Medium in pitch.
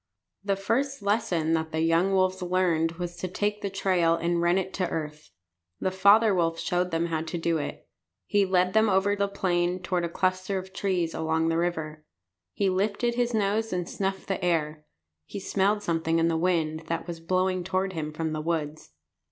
Yes: medium, 180 Hz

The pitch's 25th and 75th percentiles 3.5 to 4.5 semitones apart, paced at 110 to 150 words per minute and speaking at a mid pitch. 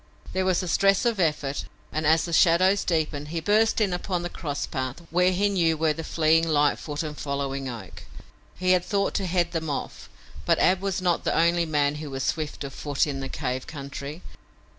No: average, 4.0 semitones; fast, 205 wpm; medium, 160 Hz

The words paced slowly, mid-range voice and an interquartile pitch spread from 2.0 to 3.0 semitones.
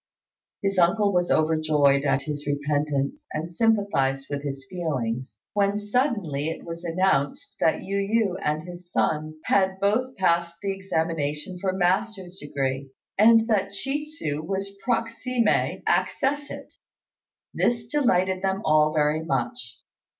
No: slow, 130 wpm; medium, 175 Hz; average, 5.3 semitones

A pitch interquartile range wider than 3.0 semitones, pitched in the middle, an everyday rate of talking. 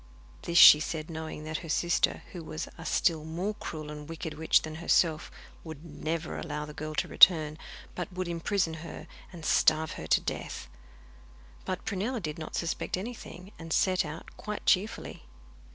No: narrow, 2.6 semitones; medium, 165 Hz; average, 170 wpm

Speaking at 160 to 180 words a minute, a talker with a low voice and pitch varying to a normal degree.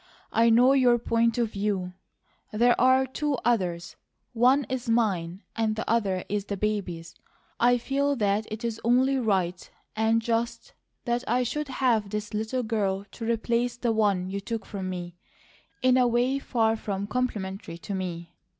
No: average, 165 wpm; high, 225 Hz; average, 3.6 semitones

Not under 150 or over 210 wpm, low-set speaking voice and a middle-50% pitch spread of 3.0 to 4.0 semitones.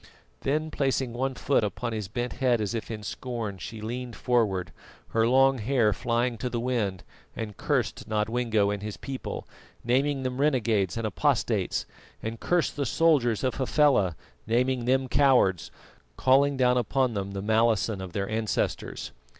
Yes: average, 160 wpm; low, 120 Hz; average, 3.5 semitones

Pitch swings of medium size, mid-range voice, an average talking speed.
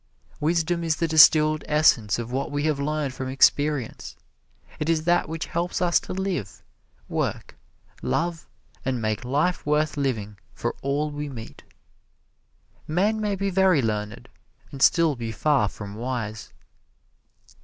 Yes: average, 5.0 semitones; medium, 150 Hz; average, 145 wpm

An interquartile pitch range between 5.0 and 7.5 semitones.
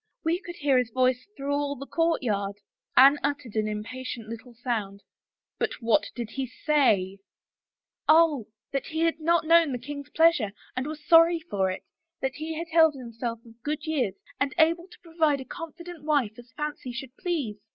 Yes: average, 5.3 semitones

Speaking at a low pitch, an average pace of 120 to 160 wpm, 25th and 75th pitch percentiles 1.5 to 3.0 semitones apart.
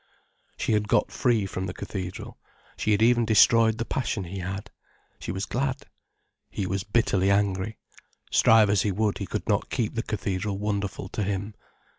No: low, 100 Hz; average, 175 wpm; narrow, 2.5 semitones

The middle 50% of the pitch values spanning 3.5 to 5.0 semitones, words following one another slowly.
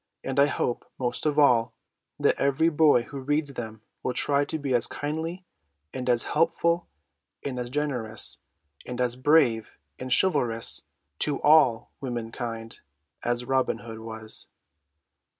No: average, 3.8 semitones; average, 145 wpm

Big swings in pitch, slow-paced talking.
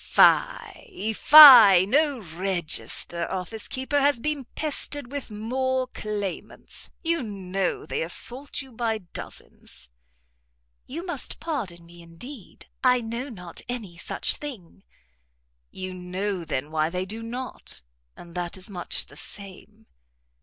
Yes: wide, 6.3 semitones; slow, 125 wpm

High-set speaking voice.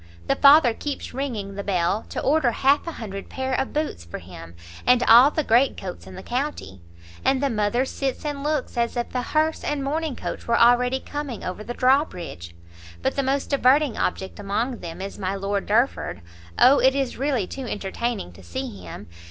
Yes: high, 245 Hz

